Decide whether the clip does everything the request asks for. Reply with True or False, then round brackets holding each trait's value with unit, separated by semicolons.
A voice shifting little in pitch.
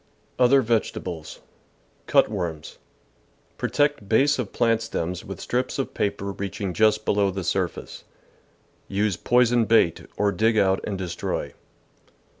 False (3.7 semitones)